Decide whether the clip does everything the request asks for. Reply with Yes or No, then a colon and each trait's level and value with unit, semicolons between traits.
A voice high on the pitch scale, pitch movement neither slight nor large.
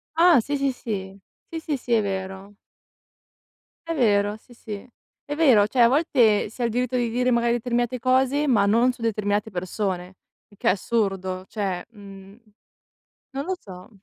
Yes: high, 225 Hz; average, 4.1 semitones